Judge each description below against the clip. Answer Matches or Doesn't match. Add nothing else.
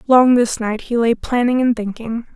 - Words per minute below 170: Doesn't match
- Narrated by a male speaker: Doesn't match